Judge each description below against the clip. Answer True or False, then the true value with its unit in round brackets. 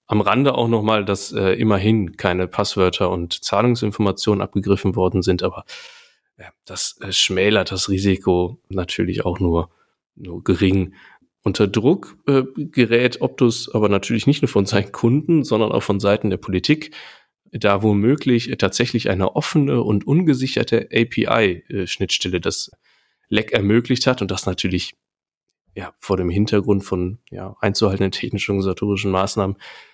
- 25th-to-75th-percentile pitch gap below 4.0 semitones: True (3.6 semitones)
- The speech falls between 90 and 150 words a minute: True (145 wpm)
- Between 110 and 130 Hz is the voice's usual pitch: False (100 Hz)